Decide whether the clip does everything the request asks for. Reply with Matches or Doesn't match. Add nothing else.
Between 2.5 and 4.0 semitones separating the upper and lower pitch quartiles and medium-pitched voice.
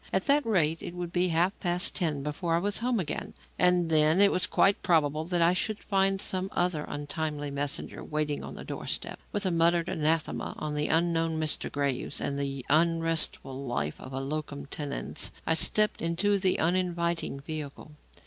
Matches